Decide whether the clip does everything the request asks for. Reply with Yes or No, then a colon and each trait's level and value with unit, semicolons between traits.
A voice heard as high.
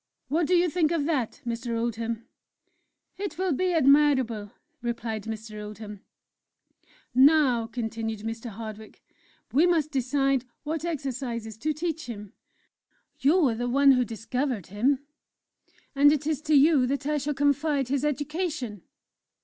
Yes: very high, 265 Hz